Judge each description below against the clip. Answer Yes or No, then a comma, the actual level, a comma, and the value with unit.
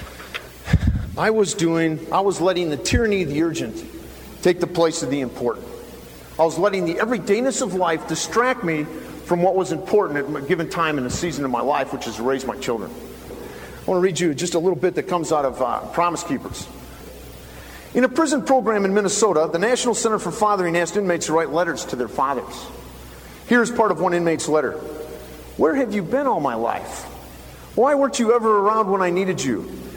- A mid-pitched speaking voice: Yes, medium, 175 Hz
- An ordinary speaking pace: No, fast, 210 wpm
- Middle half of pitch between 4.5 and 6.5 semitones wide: Yes, average, 5.1 semitones